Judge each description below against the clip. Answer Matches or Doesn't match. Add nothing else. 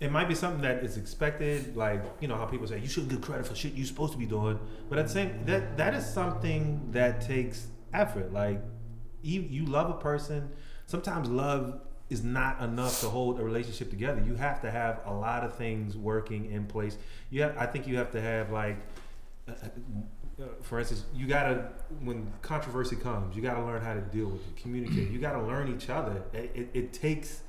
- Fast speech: Matches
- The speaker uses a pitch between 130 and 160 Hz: Doesn't match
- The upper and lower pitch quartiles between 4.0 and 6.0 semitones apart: Matches